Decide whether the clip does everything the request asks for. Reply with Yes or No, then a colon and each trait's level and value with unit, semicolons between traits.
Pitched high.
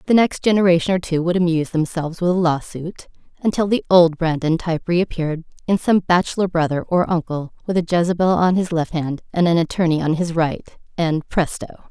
No: medium, 170 Hz